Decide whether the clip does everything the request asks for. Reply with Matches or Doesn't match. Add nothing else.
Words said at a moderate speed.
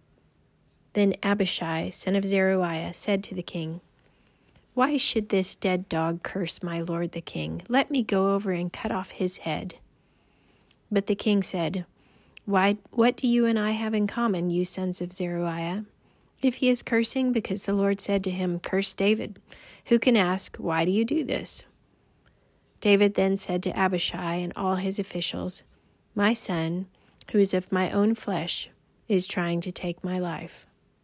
Matches